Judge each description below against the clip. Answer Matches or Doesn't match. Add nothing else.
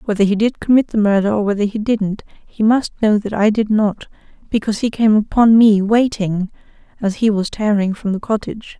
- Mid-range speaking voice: Doesn't match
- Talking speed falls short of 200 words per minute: Doesn't match